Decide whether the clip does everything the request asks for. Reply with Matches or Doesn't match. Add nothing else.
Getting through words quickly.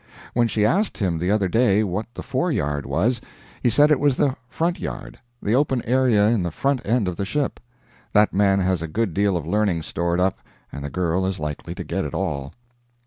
Matches